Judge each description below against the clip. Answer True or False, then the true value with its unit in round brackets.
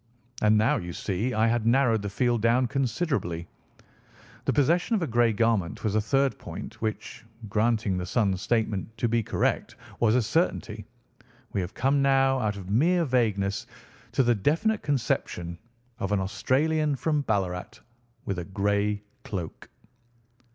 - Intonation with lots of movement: False (4.8 semitones)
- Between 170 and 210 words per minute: False (155 wpm)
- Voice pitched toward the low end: True (115 Hz)